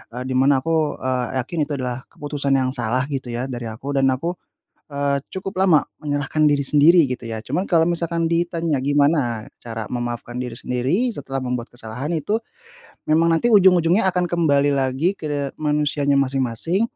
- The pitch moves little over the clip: No, average, 4.4 semitones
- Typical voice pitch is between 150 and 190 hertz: No, medium, 140 Hz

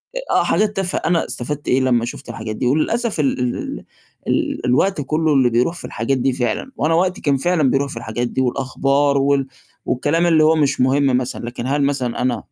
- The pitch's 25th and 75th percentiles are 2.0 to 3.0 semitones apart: No, average, 3.8 semitones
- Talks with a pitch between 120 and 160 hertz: Yes, low, 135 Hz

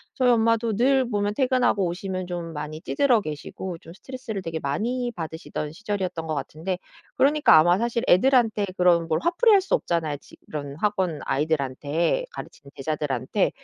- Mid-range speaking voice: Yes, medium, 180 Hz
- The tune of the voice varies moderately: No, wide, 6.8 semitones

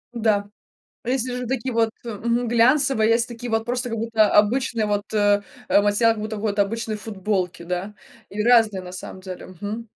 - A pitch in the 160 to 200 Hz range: No, high, 220 Hz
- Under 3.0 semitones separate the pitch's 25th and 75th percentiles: Yes, narrow, 2.4 semitones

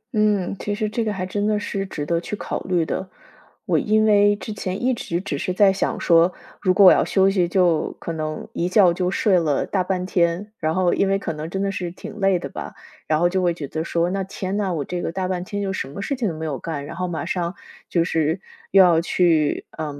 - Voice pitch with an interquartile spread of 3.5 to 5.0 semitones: No, average, 2.8 semitones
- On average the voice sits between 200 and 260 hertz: No, medium, 185 Hz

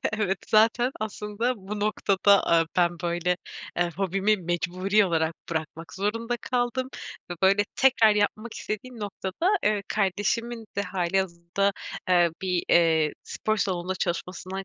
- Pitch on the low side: No, high, 195 Hz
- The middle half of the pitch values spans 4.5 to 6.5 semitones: No, average, 3.4 semitones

